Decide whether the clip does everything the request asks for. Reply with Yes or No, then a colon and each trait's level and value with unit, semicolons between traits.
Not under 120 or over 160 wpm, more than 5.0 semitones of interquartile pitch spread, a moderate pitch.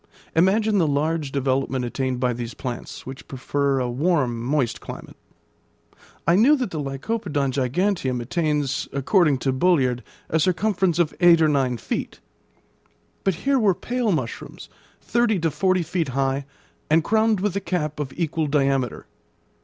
Yes: average, 150 wpm; wide, 5.6 semitones; medium, 150 Hz